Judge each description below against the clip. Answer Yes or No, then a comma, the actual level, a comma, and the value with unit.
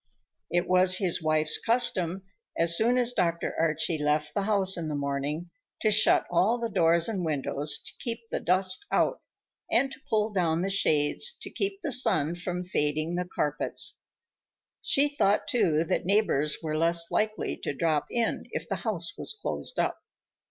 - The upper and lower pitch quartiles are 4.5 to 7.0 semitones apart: Yes, wide, 5.5 semitones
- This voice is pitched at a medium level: Yes, medium, 175 Hz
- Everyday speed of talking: Yes, average, 175 wpm